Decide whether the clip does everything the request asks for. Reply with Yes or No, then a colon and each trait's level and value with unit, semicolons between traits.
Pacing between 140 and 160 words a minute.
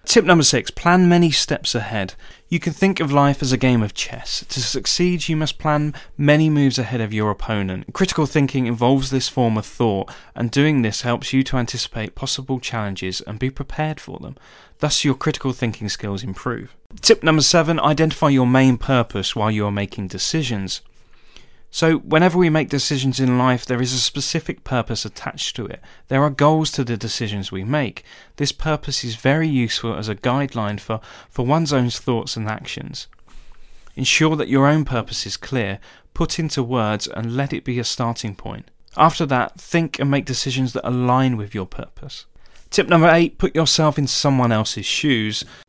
No: average, 185 wpm